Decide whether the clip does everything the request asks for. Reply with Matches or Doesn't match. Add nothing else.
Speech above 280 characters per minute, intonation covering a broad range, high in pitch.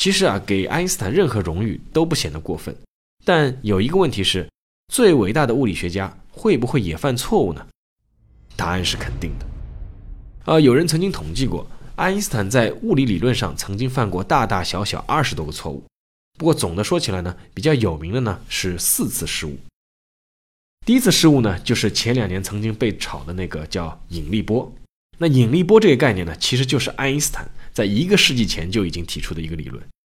Doesn't match